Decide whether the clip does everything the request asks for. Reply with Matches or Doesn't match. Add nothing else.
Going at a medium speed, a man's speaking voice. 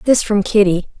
Doesn't match